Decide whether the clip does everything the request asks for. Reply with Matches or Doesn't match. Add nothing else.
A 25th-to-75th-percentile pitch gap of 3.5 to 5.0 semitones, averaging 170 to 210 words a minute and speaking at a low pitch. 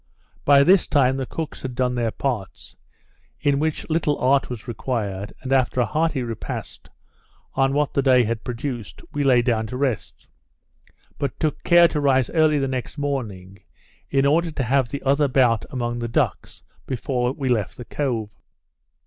Doesn't match